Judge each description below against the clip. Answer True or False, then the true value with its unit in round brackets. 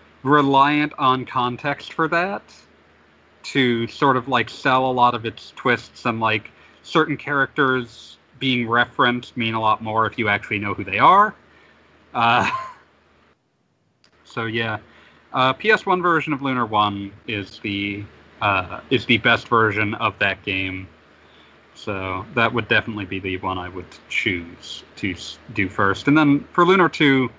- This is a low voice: True (115 Hz)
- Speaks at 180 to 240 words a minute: False (150 wpm)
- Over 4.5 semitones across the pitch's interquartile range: True (5.4 semitones)